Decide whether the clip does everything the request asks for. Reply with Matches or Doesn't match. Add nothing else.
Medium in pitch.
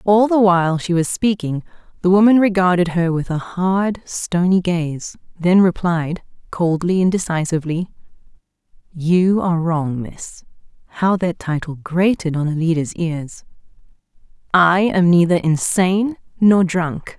Matches